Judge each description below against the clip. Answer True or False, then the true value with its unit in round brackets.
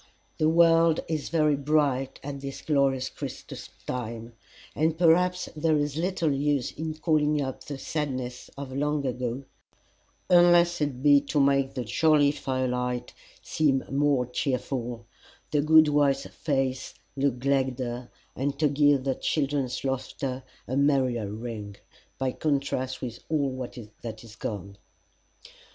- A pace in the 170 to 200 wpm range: False (135 wpm)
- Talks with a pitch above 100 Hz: True (140 Hz)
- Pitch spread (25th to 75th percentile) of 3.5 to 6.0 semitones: False (2.9 semitones)